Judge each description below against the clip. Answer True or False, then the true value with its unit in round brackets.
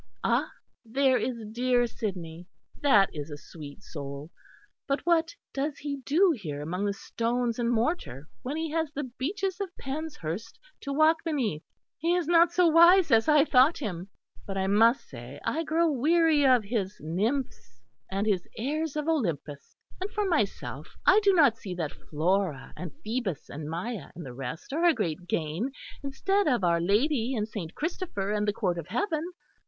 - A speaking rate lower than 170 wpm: False (175 wpm)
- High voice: True (240 Hz)